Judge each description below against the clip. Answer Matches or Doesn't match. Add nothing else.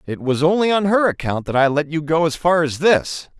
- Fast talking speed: Matches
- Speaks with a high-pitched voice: Doesn't match